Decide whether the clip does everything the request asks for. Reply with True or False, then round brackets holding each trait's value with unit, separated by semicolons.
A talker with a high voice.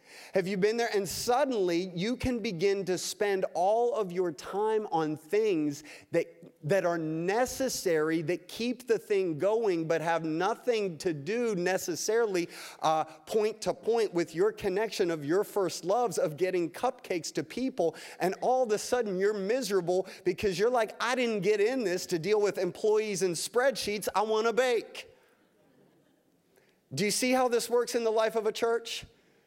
True (210 Hz)